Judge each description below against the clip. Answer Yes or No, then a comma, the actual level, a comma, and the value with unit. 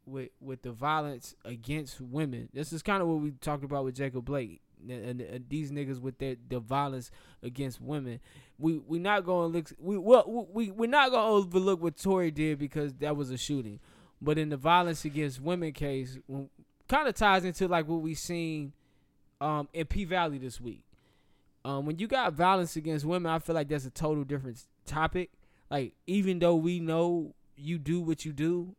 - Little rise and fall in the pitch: No, average, 4.0 semitones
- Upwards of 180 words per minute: Yes, average, 195 wpm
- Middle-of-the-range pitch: Yes, medium, 150 Hz